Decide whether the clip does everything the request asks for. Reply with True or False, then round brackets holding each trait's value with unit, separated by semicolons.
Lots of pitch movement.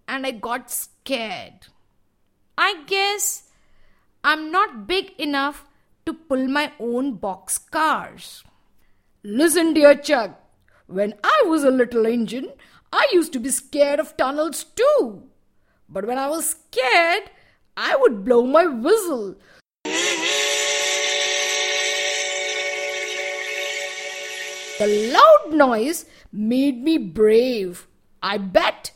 True (8.5 semitones)